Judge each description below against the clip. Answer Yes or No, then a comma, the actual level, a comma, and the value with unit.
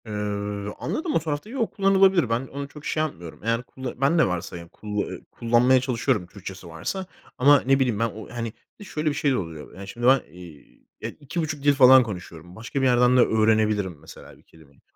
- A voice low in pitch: Yes, low, 125 Hz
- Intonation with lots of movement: Yes, wide, 6.2 semitones